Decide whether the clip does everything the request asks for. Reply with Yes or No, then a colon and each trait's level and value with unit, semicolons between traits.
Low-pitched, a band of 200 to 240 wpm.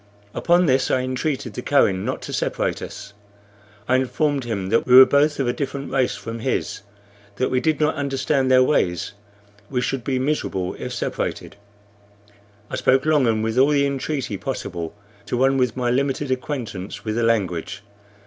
No: low, 130 Hz; average, 175 wpm